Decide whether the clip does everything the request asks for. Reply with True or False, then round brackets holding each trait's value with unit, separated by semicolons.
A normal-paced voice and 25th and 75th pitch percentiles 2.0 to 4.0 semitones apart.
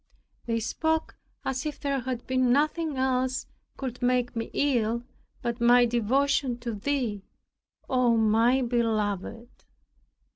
False (120 wpm; 2.4 semitones)